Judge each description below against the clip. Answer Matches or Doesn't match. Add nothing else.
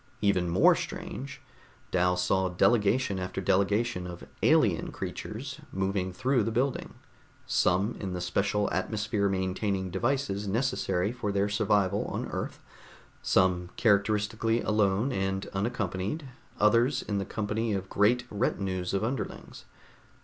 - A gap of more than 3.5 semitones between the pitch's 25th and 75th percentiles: Doesn't match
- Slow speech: Matches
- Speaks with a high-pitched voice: Doesn't match